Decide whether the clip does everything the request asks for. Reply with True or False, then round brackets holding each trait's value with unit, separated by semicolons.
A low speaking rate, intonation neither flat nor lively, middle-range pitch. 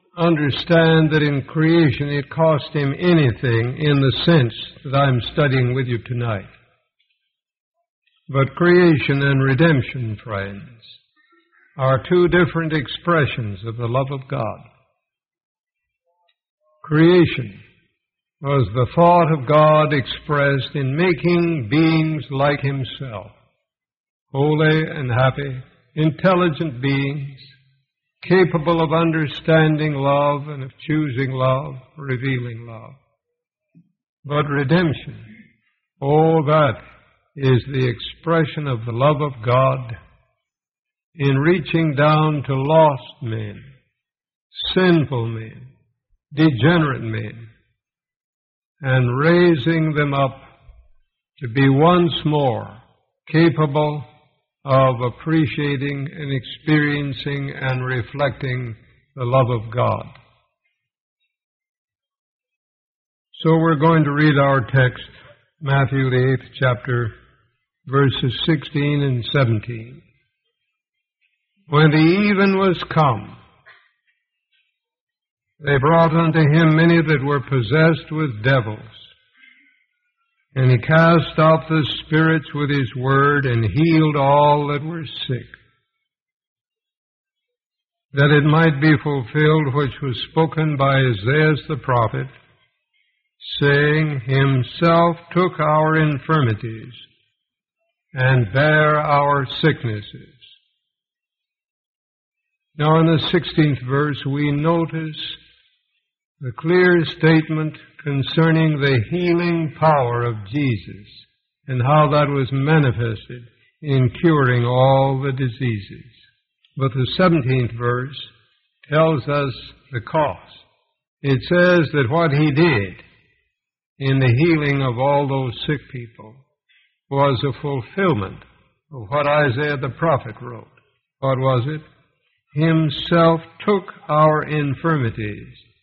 True (100 wpm; 3.7 semitones; 145 Hz)